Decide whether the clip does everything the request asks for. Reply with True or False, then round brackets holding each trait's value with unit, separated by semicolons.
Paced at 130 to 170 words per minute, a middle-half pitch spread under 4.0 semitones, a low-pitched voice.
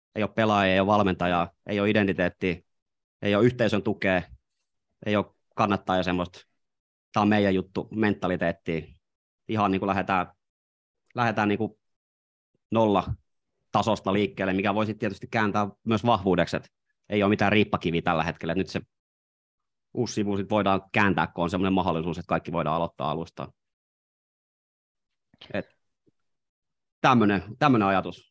True (135 wpm; 2.9 semitones; 100 Hz)